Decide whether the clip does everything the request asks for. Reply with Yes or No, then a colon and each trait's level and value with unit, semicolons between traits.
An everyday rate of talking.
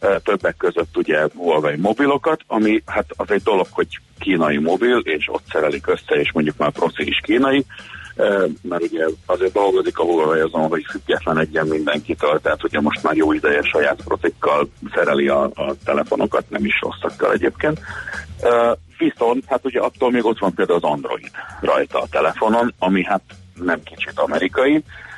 No: fast, 160 wpm